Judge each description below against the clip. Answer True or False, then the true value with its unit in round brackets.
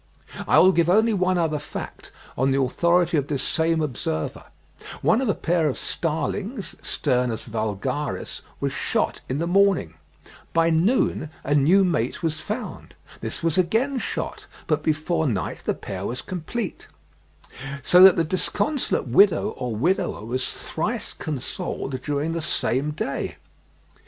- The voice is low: False (160 Hz)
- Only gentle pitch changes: False (5.5 semitones)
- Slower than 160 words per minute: True (145 wpm)